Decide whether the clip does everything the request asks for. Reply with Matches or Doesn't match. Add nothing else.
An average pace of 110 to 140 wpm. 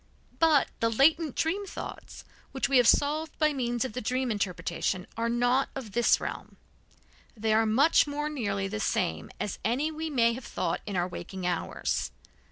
Doesn't match